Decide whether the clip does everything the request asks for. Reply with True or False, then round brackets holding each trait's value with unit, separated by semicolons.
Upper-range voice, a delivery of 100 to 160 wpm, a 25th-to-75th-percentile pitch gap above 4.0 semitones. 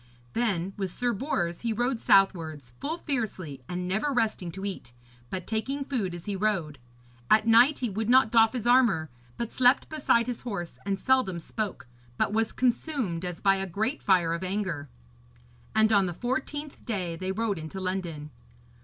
False (205 Hz; 175 wpm; 5.2 semitones)